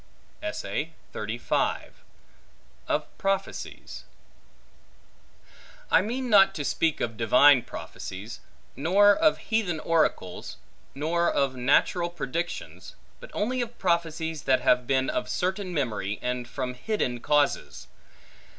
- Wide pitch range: Yes, wide, 7.3 semitones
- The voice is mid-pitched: Yes, medium, 160 Hz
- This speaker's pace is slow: Yes, slow, 105 wpm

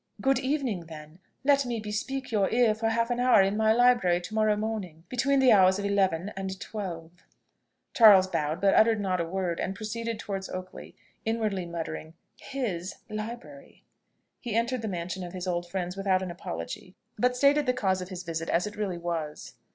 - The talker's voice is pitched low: No, high, 200 Hz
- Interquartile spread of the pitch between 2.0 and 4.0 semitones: No, average, 4.5 semitones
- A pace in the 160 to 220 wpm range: Yes, average, 190 wpm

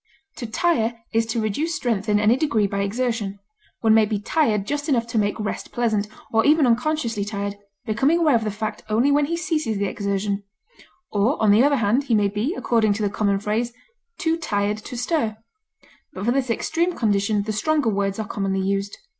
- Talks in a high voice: Yes, high, 220 Hz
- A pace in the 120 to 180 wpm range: No, fast, 205 wpm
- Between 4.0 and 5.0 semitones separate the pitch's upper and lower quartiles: Yes, average, 4.3 semitones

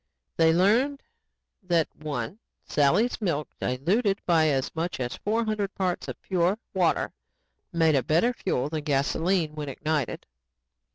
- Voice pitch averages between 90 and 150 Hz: No, medium, 165 Hz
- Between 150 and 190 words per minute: No, slow, 135 wpm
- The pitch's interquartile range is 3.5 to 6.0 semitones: Yes, average, 4.7 semitones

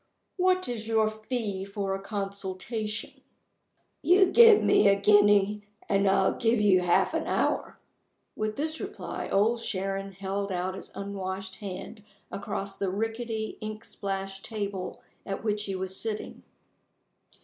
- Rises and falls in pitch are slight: Yes, narrow, 2.2 semitones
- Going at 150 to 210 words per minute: No, average, 140 wpm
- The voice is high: Yes, high, 205 Hz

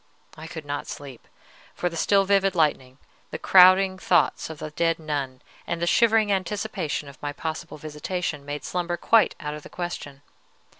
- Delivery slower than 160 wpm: No, average, 170 wpm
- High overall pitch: No, medium, 165 Hz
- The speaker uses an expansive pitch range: No, average, 4.1 semitones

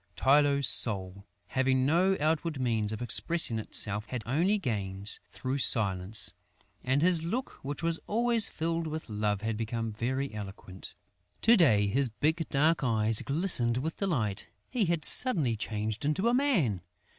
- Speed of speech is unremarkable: Yes, average, 150 wpm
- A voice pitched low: Yes, low, 130 Hz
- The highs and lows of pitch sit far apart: Yes, wide, 7.3 semitones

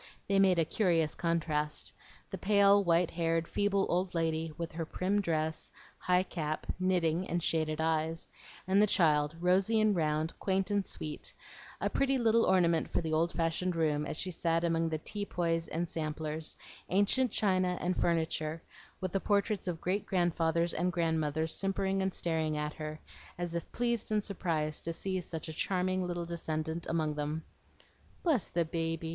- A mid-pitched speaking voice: Yes, medium, 170 Hz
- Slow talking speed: No, average, 170 wpm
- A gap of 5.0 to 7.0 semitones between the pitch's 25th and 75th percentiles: No, average, 2.8 semitones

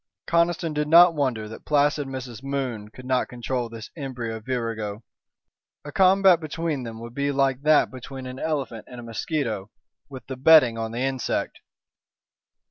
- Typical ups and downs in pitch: Yes, average, 4.2 semitones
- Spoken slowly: No, average, 160 wpm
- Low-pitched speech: Yes, low, 130 Hz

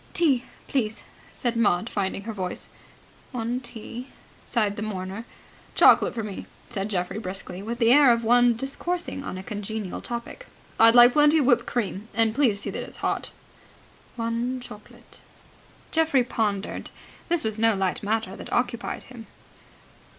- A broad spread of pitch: No, average, 3.0 semitones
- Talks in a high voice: Yes, high, 230 Hz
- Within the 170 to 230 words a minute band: No, average, 155 wpm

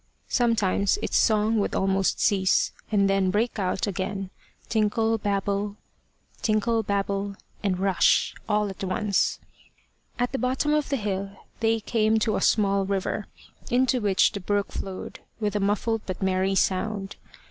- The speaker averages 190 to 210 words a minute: No, average, 140 wpm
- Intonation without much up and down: Yes, narrow, 2.2 semitones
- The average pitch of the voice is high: Yes, high, 205 Hz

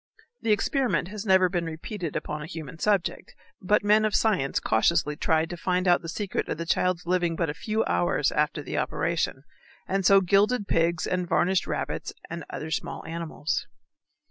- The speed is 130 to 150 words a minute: No, average, 180 wpm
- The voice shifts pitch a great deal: No, average, 3.3 semitones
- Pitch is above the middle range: No, medium, 175 Hz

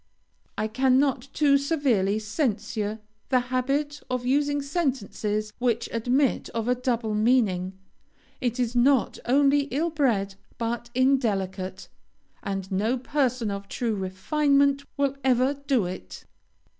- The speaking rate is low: Yes, slow, 120 wpm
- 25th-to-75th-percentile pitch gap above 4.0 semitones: Yes, average, 4.6 semitones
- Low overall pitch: No, very high, 250 Hz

